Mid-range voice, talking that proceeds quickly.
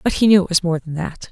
Yes: medium, 180 Hz; fast, 365 wpm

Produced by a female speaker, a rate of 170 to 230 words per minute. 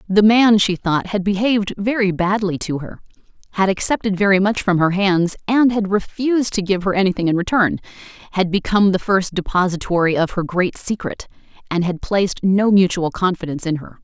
Yes: female; average, 180 wpm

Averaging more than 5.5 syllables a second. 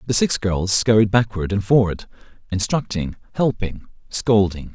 No: 4.6 syllables/s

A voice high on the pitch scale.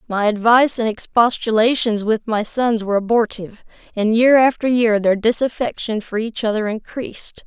Yes: high, 225 Hz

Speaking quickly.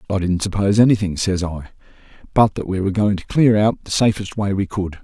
Yes: fast, 225 wpm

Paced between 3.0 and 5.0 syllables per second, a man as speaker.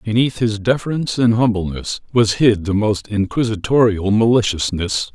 Yes: 4.9 syllables/s; male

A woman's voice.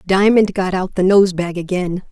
Yes: female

